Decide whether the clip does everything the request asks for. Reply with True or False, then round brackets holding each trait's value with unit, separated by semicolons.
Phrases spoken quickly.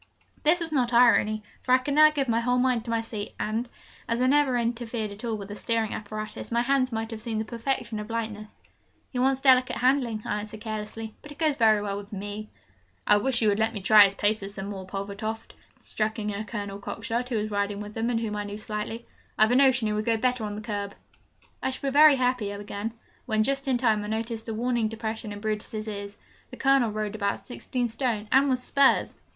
True (235 wpm)